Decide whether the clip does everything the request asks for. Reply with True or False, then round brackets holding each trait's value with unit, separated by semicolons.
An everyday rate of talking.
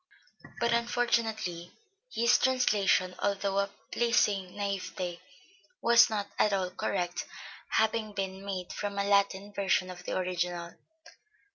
False (125 wpm)